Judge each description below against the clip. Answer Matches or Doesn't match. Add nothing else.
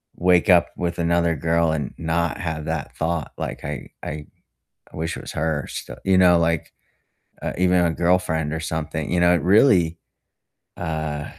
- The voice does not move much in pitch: Matches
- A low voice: Matches